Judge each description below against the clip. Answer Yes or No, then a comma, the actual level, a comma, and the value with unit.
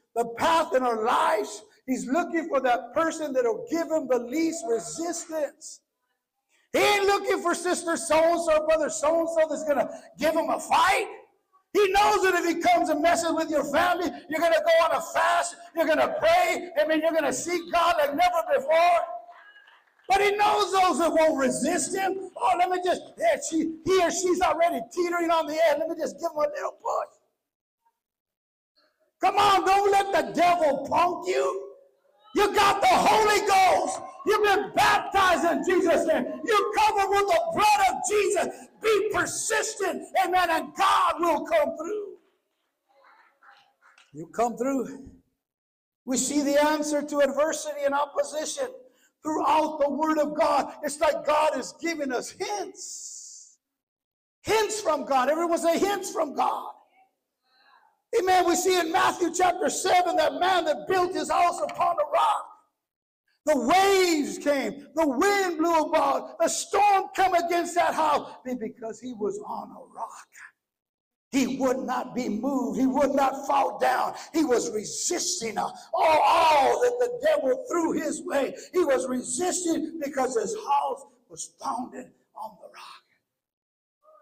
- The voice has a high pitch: Yes, very high, 330 Hz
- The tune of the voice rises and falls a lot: No, average, 3.8 semitones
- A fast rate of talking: No, average, 160 wpm